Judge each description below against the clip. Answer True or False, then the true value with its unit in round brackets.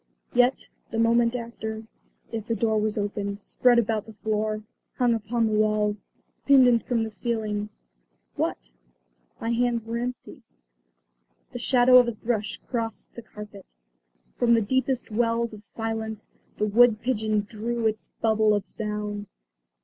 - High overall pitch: True (225 Hz)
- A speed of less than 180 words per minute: True (145 wpm)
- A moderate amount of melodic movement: False (1.9 semitones)